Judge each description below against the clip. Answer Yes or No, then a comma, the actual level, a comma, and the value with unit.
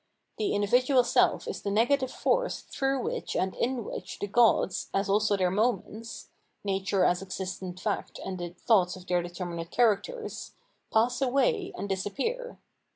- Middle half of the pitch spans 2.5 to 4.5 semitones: No, average, 5.1 semitones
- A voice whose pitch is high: Yes, high, 205 Hz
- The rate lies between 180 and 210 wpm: No, average, 155 wpm